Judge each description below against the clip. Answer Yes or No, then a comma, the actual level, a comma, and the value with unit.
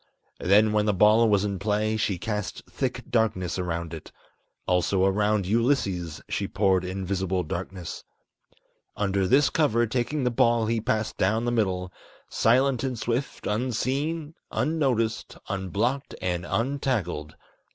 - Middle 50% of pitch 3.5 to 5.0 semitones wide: Yes, average, 4.1 semitones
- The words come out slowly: Yes, slow, 130 wpm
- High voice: No, low, 105 Hz